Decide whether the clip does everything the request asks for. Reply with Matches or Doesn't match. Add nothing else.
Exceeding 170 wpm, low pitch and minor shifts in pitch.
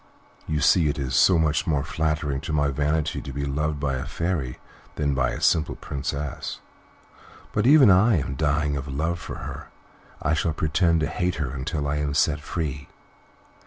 Matches